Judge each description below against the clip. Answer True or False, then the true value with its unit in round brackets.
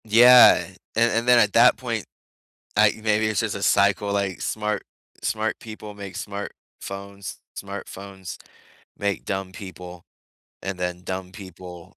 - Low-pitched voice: True (100 Hz)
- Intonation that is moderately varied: False (2.2 semitones)